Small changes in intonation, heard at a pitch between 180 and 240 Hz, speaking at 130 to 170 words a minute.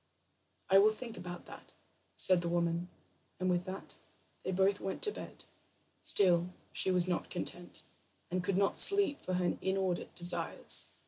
Yes: narrow, 1.6 semitones; medium, 185 Hz; average, 155 wpm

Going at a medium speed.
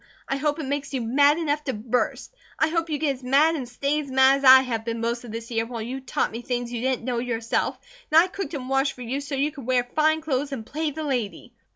No: fast, 270 wpm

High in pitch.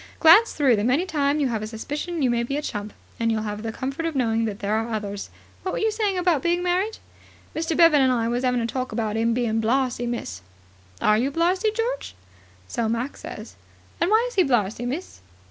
Yes: very high, 255 Hz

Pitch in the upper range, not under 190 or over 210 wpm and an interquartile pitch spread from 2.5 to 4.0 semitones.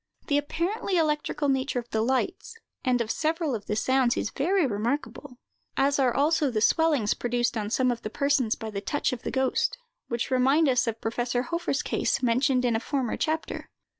Yes: very high, 260 Hz; average, 195 wpm; average, 3.7 semitones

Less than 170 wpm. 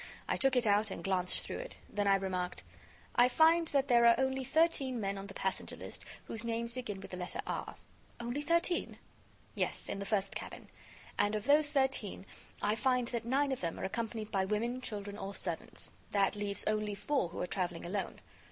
No: average, 200 wpm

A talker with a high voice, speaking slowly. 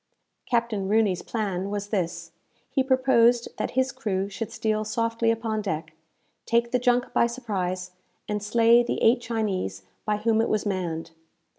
No: high, 220 Hz; average, 155 wpm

